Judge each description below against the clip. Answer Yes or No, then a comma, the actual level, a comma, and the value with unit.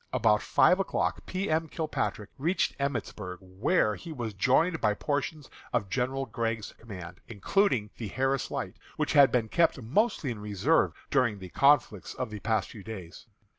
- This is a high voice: No, low, 120 Hz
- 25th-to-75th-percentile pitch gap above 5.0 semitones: Yes, wide, 5.5 semitones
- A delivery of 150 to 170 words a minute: Yes, average, 165 wpm